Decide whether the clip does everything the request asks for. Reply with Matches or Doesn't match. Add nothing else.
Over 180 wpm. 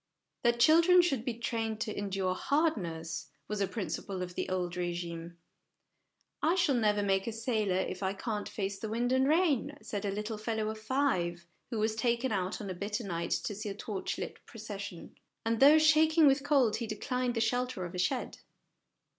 Matches